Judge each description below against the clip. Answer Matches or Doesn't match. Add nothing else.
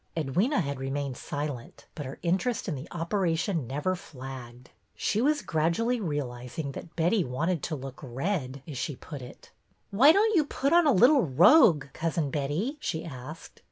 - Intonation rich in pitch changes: Matches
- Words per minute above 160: Matches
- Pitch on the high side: Doesn't match